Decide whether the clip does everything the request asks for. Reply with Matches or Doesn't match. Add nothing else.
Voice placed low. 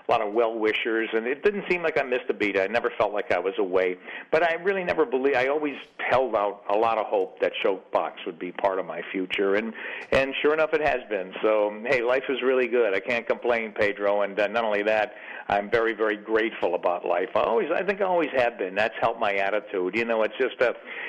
Matches